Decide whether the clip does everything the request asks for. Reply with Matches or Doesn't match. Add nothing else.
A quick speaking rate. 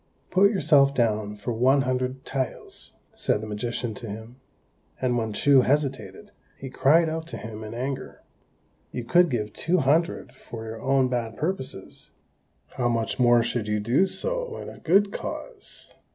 Doesn't match